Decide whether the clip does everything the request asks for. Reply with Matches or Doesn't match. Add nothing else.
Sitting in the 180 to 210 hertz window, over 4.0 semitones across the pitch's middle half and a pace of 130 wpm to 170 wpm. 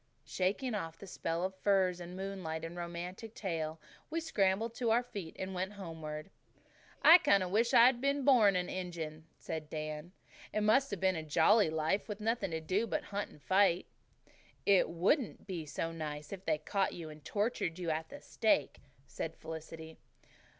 Doesn't match